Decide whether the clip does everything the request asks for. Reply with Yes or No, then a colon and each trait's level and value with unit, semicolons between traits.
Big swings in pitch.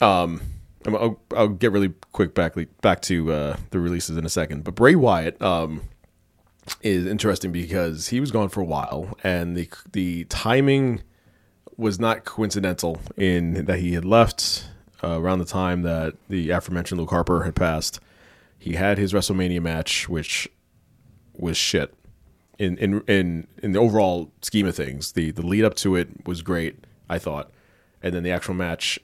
No: average, 3.0 semitones